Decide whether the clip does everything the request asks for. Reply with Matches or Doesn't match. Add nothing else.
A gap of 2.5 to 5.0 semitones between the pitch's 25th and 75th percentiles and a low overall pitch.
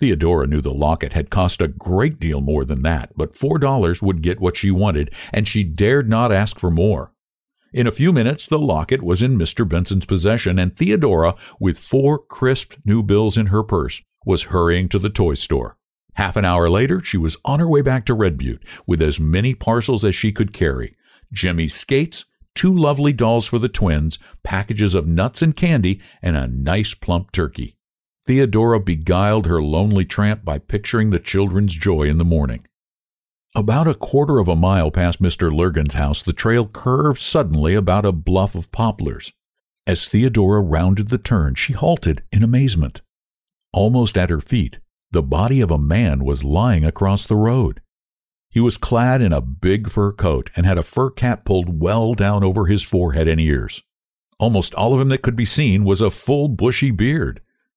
Doesn't match